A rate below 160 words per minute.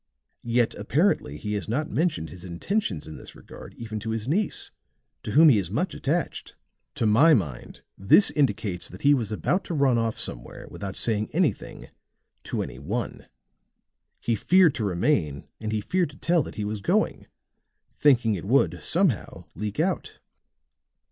No: average, 170 wpm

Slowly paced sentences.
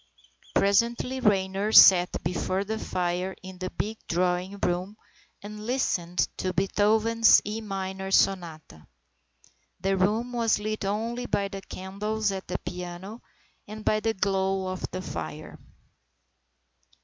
Yes: slow, 125 wpm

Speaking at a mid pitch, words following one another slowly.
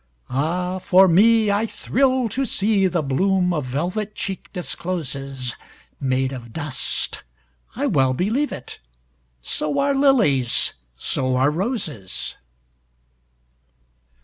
Yes: medium, 160 Hz; slow, 95 wpm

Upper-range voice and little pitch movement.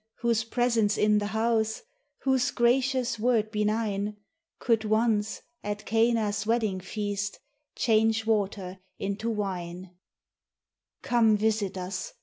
Yes: high, 215 Hz; narrow, 2.0 semitones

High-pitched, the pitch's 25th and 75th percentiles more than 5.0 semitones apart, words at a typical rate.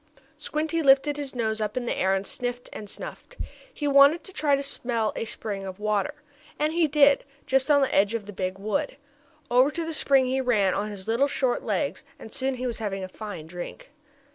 No: high, 245 Hz; wide, 5.4 semitones; fast, 220 wpm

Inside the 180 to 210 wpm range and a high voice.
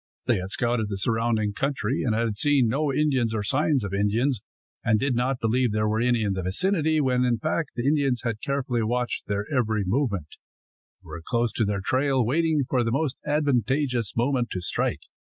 No: average, 195 wpm; low, 120 Hz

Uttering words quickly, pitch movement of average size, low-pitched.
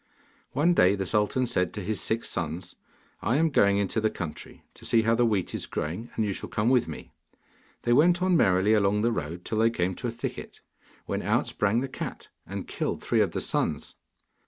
Yes: fast, 215 wpm; average, 4.0 semitones; low, 110 Hz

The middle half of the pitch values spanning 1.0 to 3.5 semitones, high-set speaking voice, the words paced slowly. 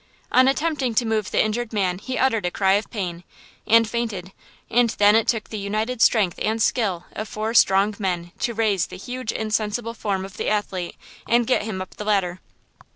No: average, 3.0 semitones; high, 215 Hz; average, 200 wpm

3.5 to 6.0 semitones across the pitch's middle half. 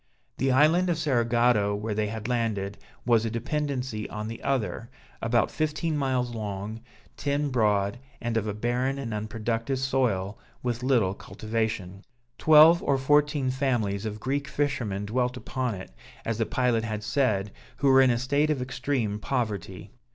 Yes: average, 3.9 semitones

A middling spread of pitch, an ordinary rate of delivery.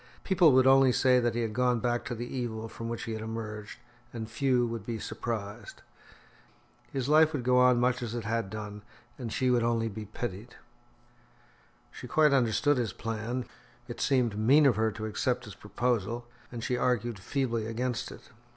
No: narrow, 2.3 semitones; average, 190 wpm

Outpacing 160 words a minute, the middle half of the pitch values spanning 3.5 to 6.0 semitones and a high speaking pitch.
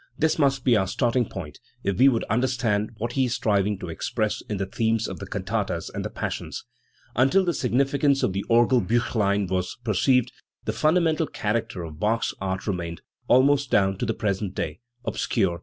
No: average, 195 wpm; average, 4.8 semitones; low, 110 Hz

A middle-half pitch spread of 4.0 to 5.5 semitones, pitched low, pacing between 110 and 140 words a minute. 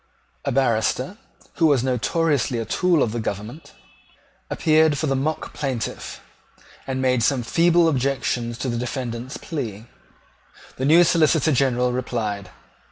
Yes: average, 4.6 semitones; low, 130 Hz; slow, 135 wpm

